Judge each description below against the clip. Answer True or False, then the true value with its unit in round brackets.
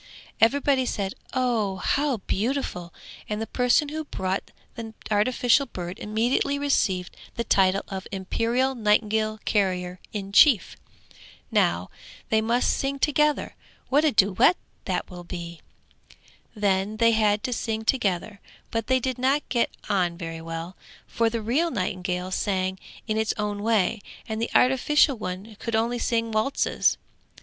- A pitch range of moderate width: True (4.7 semitones)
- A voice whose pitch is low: False (220 Hz)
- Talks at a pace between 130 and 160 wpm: True (140 wpm)